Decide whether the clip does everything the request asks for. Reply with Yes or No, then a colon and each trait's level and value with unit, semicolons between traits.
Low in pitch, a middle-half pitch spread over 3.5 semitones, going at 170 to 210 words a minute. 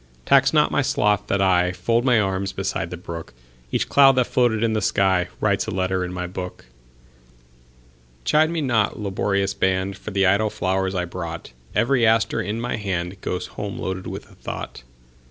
No: very low, 95 Hz; average, 4.5 semitones; average, 155 wpm